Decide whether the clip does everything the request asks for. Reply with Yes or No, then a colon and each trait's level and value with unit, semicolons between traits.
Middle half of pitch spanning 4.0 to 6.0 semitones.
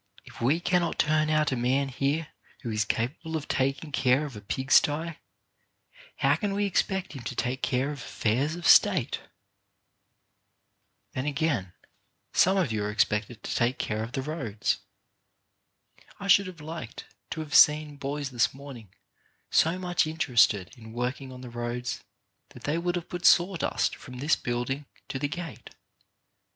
Yes: average, 4.7 semitones